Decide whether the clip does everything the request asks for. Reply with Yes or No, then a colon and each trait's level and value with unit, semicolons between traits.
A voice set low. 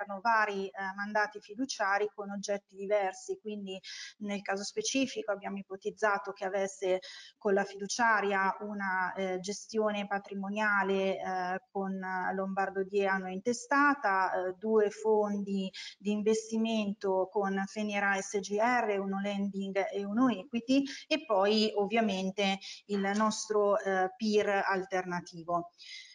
No: high, 200 Hz